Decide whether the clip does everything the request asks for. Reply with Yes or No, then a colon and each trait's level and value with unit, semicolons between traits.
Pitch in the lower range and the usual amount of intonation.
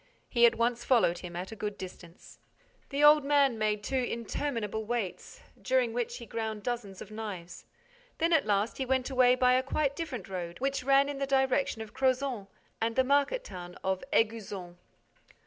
No: high, 235 Hz; average, 4.4 semitones